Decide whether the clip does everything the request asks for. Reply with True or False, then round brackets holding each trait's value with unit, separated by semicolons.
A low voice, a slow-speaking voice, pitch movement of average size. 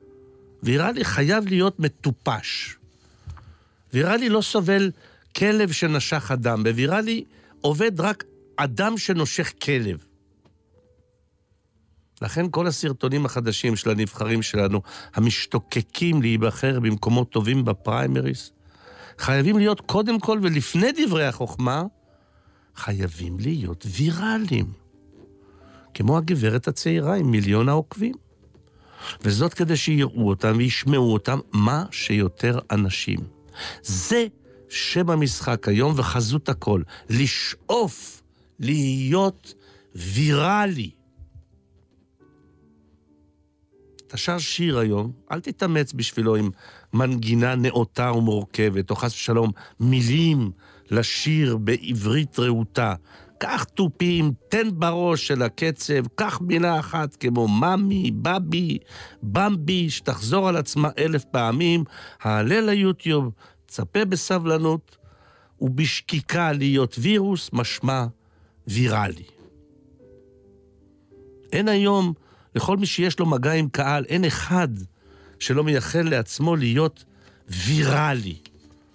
False (130 Hz; 95 wpm; 8.0 semitones)